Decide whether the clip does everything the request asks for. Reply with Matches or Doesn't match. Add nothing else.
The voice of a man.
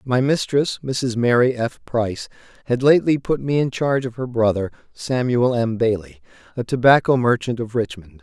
Matches